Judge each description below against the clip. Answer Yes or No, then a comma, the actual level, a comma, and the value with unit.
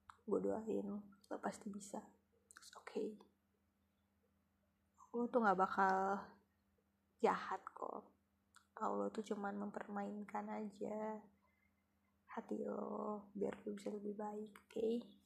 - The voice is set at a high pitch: Yes, high, 200 Hz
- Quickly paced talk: No, average, 105 wpm